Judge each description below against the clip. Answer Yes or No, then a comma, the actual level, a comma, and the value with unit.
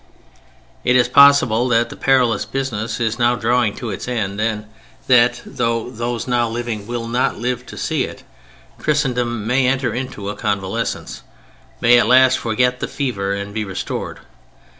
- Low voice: Yes, low, 120 Hz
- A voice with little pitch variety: Yes, narrow, 2.2 semitones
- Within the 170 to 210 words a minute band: No, average, 160 wpm